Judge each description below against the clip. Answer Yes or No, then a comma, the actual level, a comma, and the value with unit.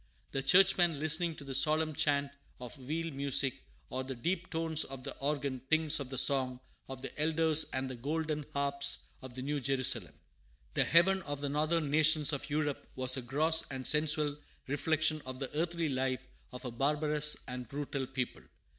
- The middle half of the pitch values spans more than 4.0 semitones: No, average, 3.0 semitones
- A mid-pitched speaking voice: Yes, medium, 145 Hz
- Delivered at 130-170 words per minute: No, average, 180 wpm